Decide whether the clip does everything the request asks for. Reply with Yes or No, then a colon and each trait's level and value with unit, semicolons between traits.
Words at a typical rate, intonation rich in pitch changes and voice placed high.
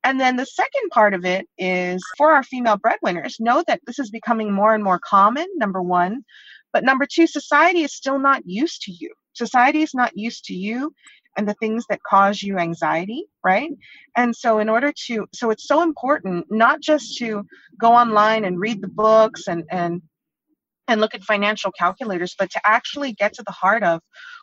Yes: average, 195 wpm; wide, 6.0 semitones; high, 225 Hz